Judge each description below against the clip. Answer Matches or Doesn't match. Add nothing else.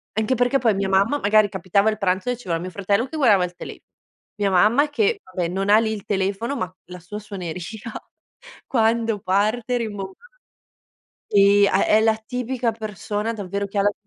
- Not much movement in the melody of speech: Doesn't match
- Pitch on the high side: Matches